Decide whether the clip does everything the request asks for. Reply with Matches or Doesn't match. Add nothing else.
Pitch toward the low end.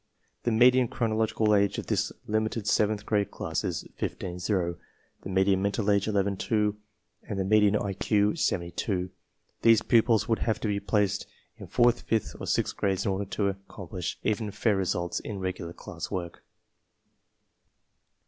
Matches